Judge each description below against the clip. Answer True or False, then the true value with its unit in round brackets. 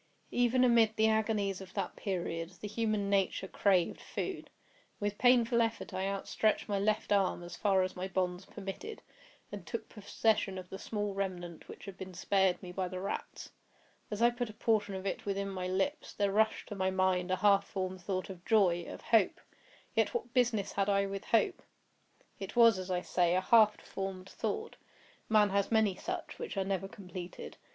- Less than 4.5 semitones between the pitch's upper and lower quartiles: True (2.6 semitones)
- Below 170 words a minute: False (185 wpm)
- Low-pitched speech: False (195 Hz)